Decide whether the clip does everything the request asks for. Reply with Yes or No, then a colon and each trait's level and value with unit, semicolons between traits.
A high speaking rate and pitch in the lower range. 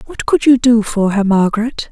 No: fast, 220 wpm; high, 230 Hz